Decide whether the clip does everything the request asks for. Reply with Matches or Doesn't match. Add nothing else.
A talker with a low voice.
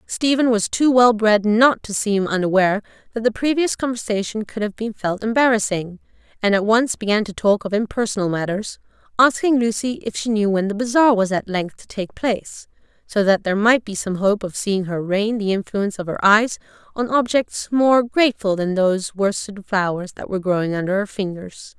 Doesn't match